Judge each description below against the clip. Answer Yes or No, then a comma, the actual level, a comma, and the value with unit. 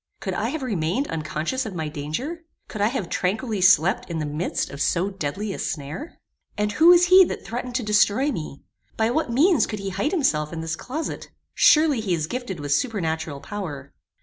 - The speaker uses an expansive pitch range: Yes, wide, 8.3 semitones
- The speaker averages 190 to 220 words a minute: Yes, average, 200 wpm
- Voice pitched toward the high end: Yes, high, 200 Hz